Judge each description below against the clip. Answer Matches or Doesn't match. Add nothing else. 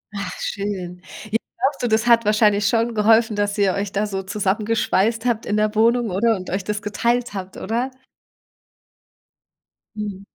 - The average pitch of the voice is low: Doesn't match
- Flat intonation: Matches